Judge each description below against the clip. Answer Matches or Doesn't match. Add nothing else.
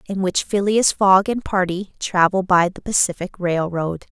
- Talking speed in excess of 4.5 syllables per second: Doesn't match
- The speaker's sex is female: Matches